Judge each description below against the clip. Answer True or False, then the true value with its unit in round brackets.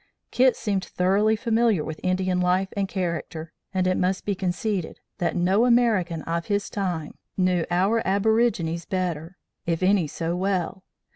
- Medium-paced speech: True (150 wpm)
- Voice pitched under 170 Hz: False (185 Hz)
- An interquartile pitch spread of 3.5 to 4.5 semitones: False (2.6 semitones)